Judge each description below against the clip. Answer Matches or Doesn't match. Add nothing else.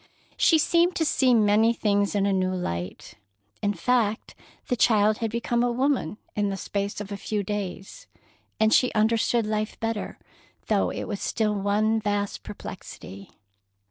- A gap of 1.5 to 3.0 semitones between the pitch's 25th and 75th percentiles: Matches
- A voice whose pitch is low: Doesn't match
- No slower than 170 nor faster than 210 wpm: Doesn't match